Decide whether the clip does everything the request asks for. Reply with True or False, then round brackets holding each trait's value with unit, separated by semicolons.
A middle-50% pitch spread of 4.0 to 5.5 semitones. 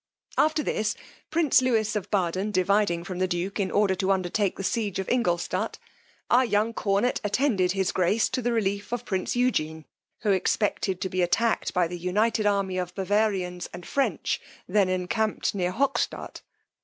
False (3.2 semitones)